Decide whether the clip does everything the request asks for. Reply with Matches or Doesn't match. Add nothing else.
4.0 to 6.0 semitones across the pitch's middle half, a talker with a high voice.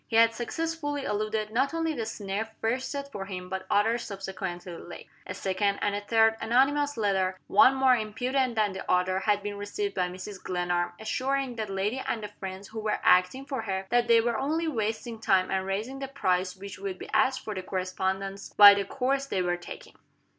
Matches